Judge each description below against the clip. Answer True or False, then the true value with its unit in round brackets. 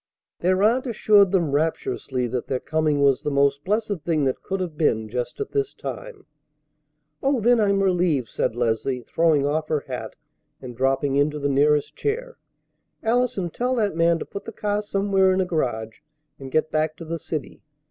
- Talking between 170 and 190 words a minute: True (185 wpm)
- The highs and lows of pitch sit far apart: True (6.4 semitones)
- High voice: False (160 Hz)